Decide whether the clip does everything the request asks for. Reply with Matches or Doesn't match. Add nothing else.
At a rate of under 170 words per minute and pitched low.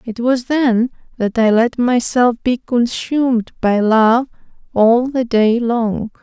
Doesn't match